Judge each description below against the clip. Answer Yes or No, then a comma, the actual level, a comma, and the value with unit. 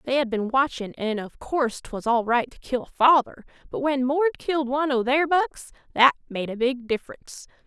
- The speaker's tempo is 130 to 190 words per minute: No, fast, 205 wpm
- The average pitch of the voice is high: Yes, very high, 260 Hz